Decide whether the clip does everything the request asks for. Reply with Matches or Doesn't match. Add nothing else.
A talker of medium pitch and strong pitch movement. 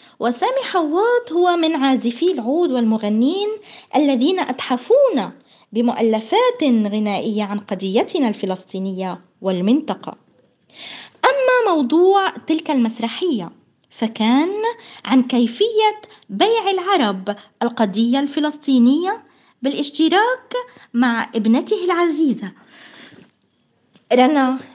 Doesn't match